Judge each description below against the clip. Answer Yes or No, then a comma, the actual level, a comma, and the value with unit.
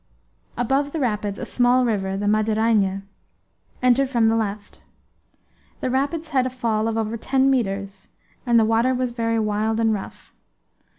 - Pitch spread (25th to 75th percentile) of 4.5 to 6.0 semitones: No, average, 3.0 semitones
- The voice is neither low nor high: No, high, 225 Hz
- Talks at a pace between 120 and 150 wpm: No, average, 160 wpm